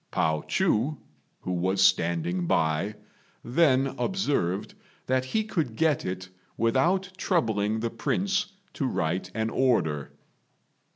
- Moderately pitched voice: No, low, 115 Hz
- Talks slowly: Yes, slow, 115 wpm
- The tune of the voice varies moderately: No, wide, 8.6 semitones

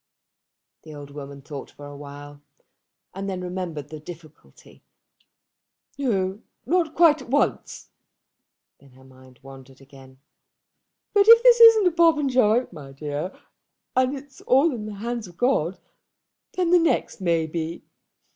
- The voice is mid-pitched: Yes, medium, 180 Hz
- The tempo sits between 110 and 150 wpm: Yes, average, 140 wpm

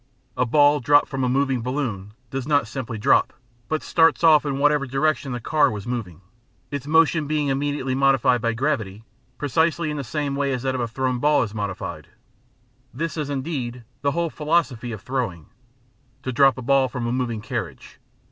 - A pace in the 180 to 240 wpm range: Yes, average, 185 wpm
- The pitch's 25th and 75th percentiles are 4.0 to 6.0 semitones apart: No, average, 3.3 semitones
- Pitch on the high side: No, low, 135 Hz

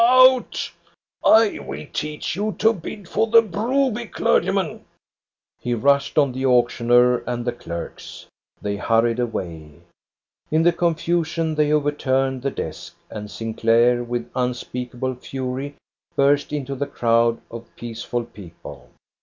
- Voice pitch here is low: Yes, low, 130 Hz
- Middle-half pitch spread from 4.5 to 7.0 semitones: Yes, average, 5.1 semitones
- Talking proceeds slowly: Yes, slow, 130 wpm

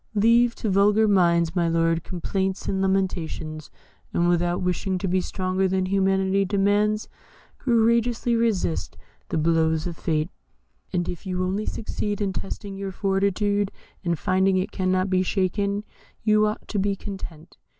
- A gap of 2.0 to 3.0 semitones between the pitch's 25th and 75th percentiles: Yes, narrow, 2.5 semitones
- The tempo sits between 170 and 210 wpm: No, average, 150 wpm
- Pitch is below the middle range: No, high, 190 Hz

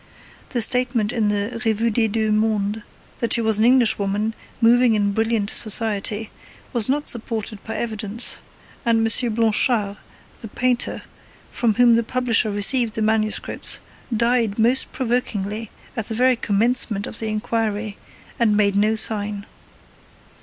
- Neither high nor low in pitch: No, high, 225 Hz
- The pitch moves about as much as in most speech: No, narrow, 2.0 semitones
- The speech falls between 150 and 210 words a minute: No, average, 140 wpm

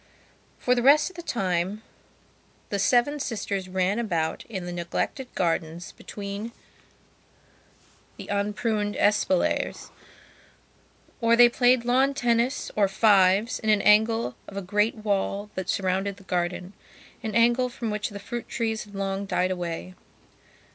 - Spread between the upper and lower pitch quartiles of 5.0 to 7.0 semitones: No, average, 3.7 semitones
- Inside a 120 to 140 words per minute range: Yes, slow, 135 wpm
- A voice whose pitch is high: Yes, high, 205 Hz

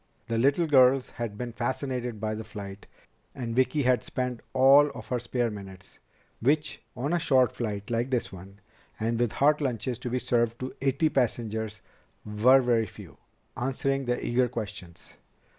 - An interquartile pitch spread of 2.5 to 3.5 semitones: Yes, average, 2.9 semitones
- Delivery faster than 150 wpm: Yes, average, 165 wpm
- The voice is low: Yes, low, 120 Hz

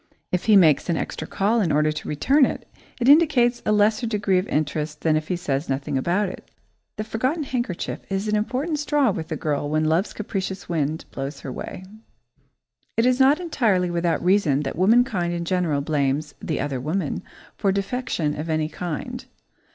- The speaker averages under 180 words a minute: No, average, 185 wpm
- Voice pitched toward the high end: No, medium, 180 Hz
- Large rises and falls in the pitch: Yes, wide, 6.2 semitones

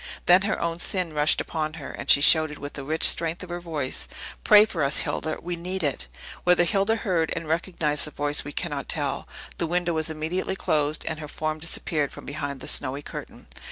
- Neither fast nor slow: No, fast, 210 wpm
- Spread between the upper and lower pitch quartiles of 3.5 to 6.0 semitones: No, average, 2.8 semitones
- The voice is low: No, medium, 160 Hz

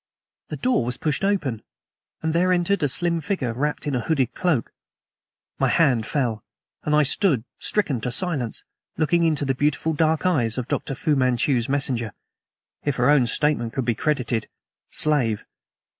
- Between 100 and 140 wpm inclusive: No, average, 165 wpm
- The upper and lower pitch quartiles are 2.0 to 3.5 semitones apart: No, average, 4.7 semitones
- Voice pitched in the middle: Yes, medium, 145 Hz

